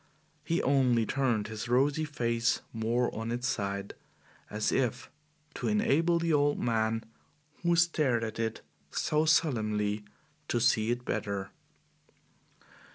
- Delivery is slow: Yes, slow, 125 wpm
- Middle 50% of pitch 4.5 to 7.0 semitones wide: Yes, average, 4.8 semitones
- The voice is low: Yes, low, 120 Hz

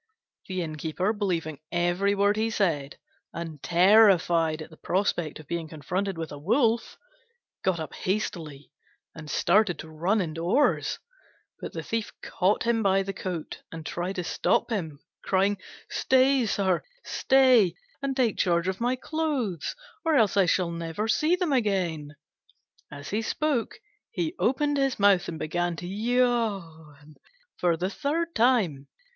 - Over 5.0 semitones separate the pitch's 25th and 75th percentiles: Yes, wide, 5.5 semitones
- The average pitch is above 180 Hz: Yes, high, 190 Hz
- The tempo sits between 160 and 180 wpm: No, average, 150 wpm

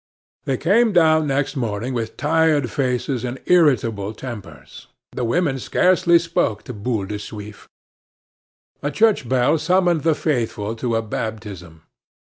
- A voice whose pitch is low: Yes, low, 125 Hz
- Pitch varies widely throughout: Yes, wide, 6.5 semitones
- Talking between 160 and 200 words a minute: No, slow, 135 wpm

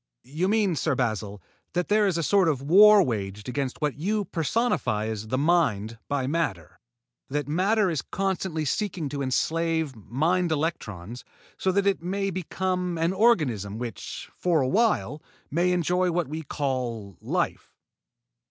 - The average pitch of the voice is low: No, medium, 160 Hz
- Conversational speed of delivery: Yes, average, 150 wpm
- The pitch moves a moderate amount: No, wide, 6.3 semitones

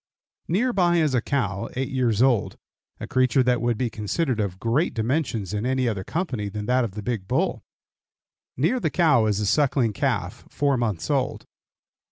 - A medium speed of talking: Yes, average, 185 wpm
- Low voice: Yes, low, 125 Hz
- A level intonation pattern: No, average, 4.8 semitones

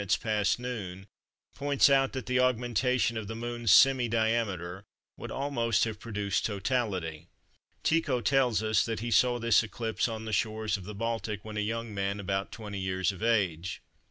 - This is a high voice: No, low, 110 Hz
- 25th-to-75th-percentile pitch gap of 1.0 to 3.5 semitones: Yes, average, 3.1 semitones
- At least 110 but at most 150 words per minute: No, average, 170 wpm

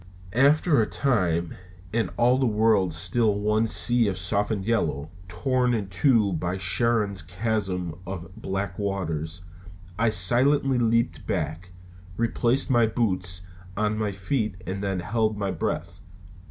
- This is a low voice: Yes, low, 100 Hz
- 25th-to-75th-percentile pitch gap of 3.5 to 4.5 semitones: Yes, average, 4.2 semitones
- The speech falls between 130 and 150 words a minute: Yes, slow, 135 wpm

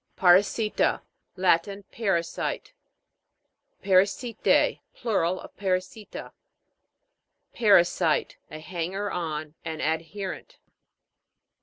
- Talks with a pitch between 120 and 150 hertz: No, medium, 185 Hz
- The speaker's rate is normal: No, slow, 70 wpm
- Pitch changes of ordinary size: Yes, average, 3.5 semitones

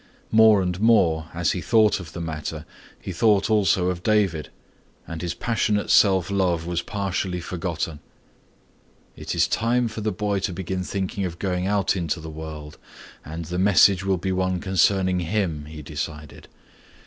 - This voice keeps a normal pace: Yes, average, 165 wpm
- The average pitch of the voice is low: Yes, very low, 90 Hz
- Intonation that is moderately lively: Yes, average, 3.2 semitones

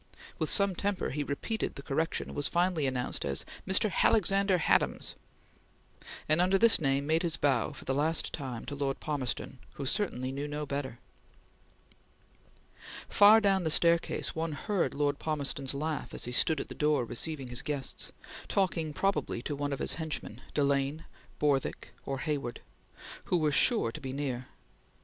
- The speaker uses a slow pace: No, average, 165 wpm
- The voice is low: No, medium, 150 Hz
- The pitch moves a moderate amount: Yes, average, 3.7 semitones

